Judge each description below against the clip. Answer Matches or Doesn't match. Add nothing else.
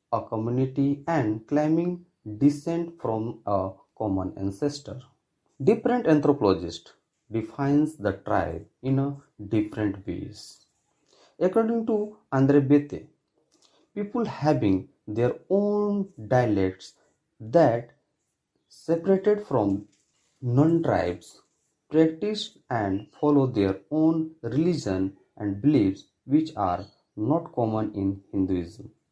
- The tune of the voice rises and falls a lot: Matches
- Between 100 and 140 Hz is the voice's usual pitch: Matches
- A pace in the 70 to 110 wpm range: Matches